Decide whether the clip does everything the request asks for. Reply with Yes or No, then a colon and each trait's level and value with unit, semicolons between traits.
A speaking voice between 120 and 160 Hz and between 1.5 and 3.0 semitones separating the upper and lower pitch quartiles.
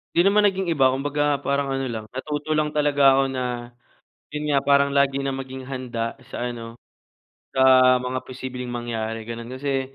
Yes: low, 135 Hz; narrow, 2.5 semitones